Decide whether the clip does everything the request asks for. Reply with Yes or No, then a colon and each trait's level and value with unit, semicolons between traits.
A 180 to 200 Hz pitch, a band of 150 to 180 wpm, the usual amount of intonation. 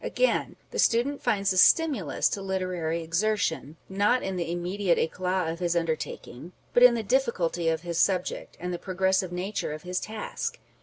Yes: medium, 185 Hz; average, 170 wpm; average, 3.2 semitones